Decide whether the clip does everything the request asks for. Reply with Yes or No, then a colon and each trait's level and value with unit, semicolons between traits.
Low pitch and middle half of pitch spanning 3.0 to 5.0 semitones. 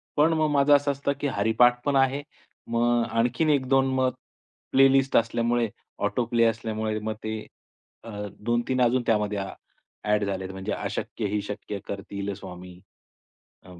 Yes: low, 115 Hz; average, 4.2 semitones